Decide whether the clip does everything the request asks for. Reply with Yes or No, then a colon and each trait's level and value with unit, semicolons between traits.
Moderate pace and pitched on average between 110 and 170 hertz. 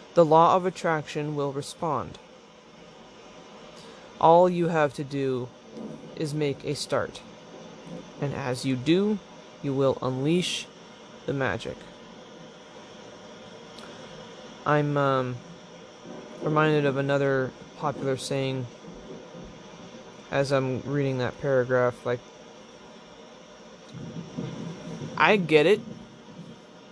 No: slow, 90 wpm; medium, 140 Hz